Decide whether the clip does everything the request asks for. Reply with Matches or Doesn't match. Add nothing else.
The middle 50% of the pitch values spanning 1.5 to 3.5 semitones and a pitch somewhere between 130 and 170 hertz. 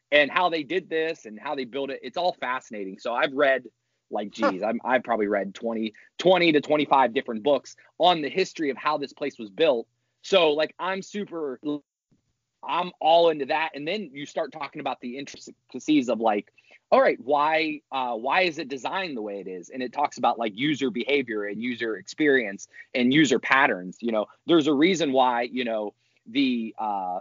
Doesn't match